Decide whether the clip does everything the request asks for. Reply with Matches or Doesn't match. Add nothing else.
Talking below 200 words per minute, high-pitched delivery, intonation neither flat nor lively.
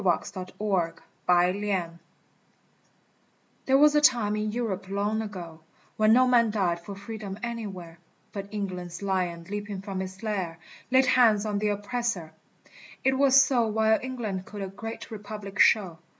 Matches